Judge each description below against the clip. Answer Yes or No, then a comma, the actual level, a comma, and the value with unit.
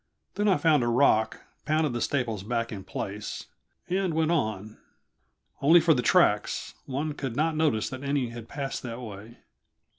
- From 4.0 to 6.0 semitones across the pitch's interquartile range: Yes, average, 5.1 semitones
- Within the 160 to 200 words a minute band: Yes, average, 170 wpm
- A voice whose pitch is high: No, low, 130 Hz